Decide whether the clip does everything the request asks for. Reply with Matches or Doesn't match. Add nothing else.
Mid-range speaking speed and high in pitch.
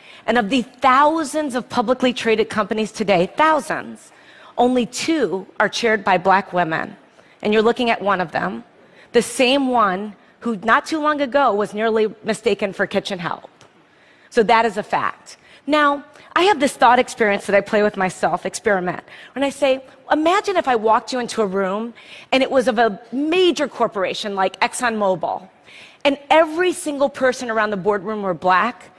Matches